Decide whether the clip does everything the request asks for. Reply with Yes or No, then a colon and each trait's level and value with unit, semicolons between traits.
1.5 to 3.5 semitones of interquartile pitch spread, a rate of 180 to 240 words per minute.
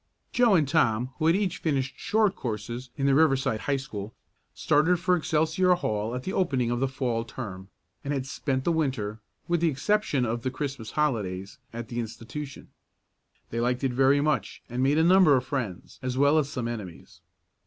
No: average, 4.8 semitones; average, 190 wpm